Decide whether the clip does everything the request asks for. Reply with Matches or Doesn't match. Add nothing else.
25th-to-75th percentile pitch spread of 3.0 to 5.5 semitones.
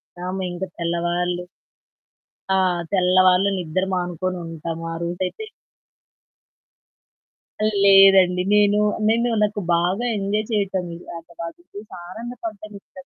Doesn't match